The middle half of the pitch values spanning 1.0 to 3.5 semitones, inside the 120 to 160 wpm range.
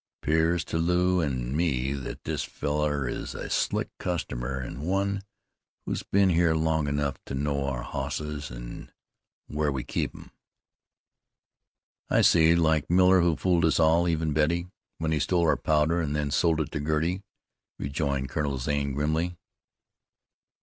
Yes: average, 3.2 semitones; average, 155 wpm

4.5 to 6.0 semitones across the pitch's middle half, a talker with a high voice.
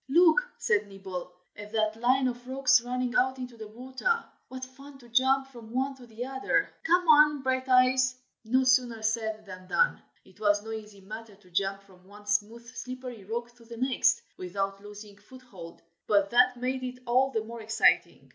No: average, 3.7 semitones; high, 240 Hz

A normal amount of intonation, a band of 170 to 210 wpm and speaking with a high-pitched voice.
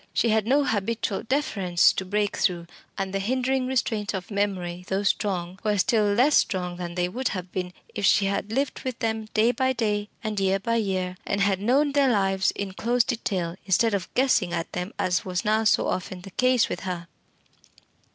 Yes: average, 3.7 semitones; average, 200 wpm; high, 205 Hz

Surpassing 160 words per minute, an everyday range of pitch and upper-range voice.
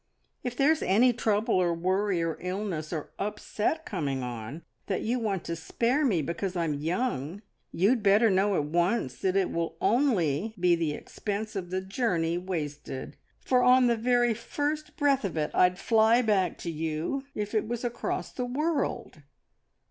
No: average, 170 wpm; wide, 6.1 semitones; high, 195 Hz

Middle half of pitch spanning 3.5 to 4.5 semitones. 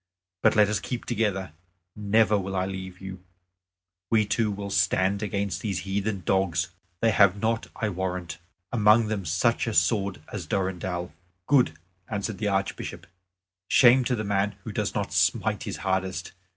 No: narrow, 2.4 semitones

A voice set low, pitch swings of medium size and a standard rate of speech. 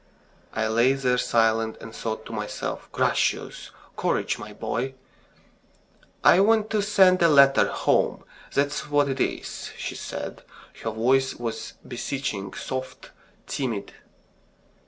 No: low, 130 Hz; average, 4.2 semitones; slow, 125 wpm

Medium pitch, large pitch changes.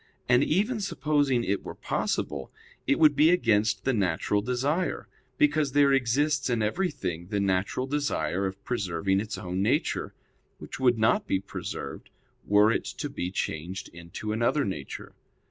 No: low, 110 Hz; wide, 6.8 semitones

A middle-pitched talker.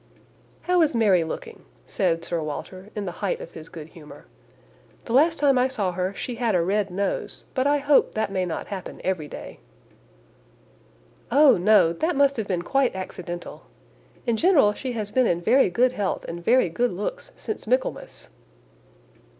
No: high, 210 Hz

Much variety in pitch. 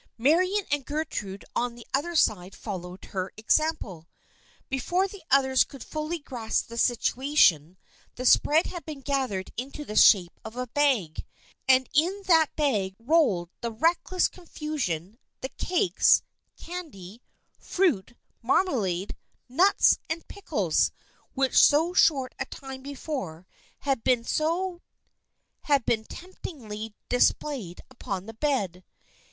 Yes: wide, 6.6 semitones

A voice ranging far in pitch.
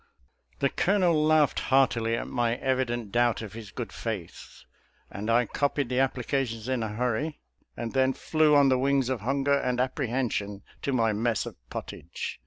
No: average, 3.2 semitones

